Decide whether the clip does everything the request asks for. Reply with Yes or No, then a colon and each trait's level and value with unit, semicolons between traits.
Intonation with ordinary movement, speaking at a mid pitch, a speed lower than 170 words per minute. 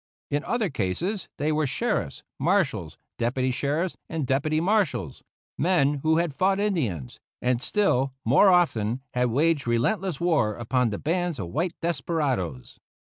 No: wide, 6.1 semitones; medium, 145 Hz; average, 140 wpm